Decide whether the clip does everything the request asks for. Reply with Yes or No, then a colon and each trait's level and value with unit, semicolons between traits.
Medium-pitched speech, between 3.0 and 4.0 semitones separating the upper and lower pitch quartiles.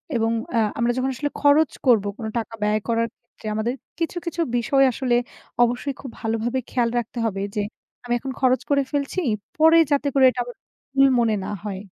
No: high, 245 Hz; average, 3.5 semitones